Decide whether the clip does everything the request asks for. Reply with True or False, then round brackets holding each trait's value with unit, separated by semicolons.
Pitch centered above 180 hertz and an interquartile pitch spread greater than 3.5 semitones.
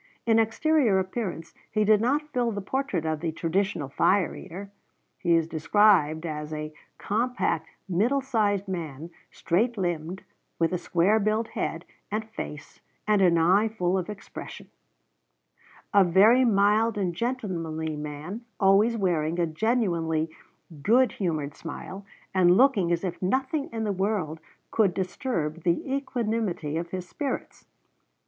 True (190 Hz; 4.9 semitones)